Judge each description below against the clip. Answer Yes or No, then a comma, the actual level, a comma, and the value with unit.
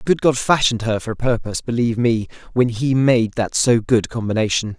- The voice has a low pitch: Yes, low, 120 Hz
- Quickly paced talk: Yes, fast, 215 wpm